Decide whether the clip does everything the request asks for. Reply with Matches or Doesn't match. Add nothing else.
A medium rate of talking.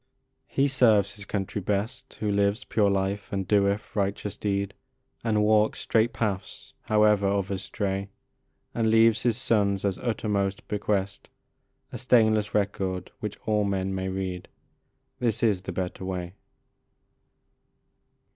Doesn't match